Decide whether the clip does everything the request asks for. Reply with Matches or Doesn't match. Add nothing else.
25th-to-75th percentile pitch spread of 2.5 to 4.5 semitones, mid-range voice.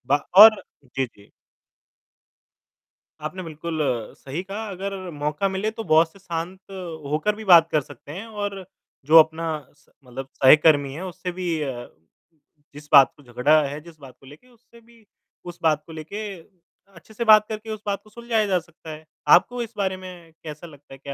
Doesn't match